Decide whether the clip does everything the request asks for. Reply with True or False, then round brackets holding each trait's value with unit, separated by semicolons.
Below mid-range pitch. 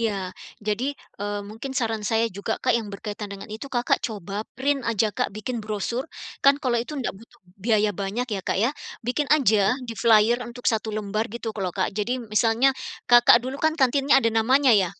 False (230 Hz)